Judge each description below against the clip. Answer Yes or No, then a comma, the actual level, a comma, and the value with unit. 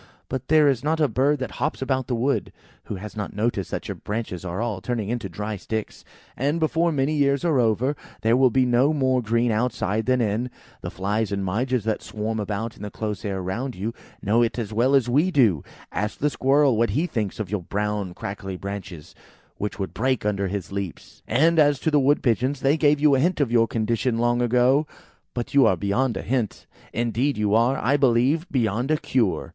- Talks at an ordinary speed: No, fast, 215 wpm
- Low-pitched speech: Yes, low, 120 Hz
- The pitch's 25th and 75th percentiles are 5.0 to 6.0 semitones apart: No, average, 4.4 semitones